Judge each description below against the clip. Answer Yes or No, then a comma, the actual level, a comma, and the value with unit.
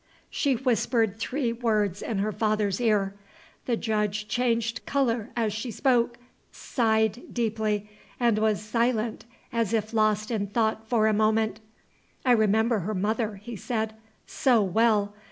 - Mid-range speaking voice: No, high, 220 Hz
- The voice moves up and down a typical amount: No, narrow, 1.8 semitones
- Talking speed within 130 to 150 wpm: Yes, average, 140 wpm